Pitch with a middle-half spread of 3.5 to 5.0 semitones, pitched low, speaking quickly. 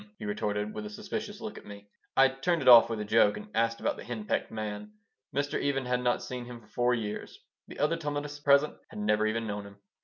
Yes: average, 4.2 semitones; low, 115 Hz; fast, 240 wpm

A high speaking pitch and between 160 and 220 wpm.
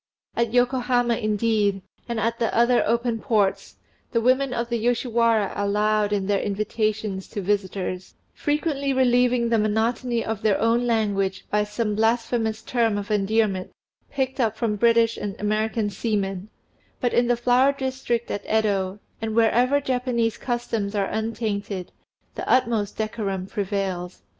No: high, 225 Hz; average, 145 wpm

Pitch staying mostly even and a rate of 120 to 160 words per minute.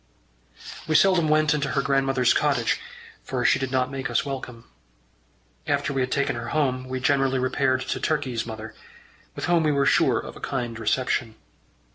No: narrow, 1.9 semitones; average, 175 wpm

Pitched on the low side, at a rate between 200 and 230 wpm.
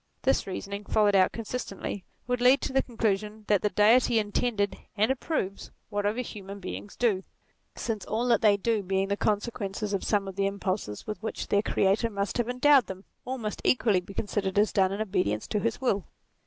No: high, 205 Hz; fast, 205 wpm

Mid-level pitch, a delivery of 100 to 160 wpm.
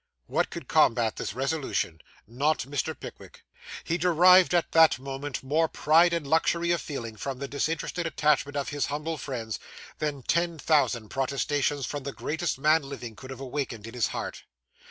No: medium, 145 Hz; average, 170 wpm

